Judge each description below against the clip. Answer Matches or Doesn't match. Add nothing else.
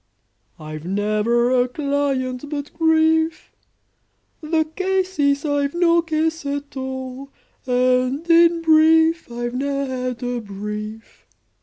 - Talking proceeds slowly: Matches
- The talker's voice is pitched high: Matches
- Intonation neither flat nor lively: Matches